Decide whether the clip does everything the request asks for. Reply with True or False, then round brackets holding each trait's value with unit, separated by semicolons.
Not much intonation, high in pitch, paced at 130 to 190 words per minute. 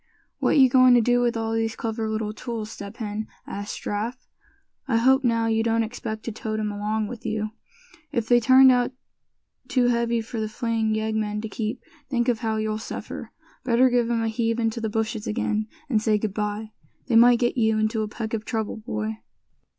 False (1.7 semitones; 225 Hz; 205 wpm)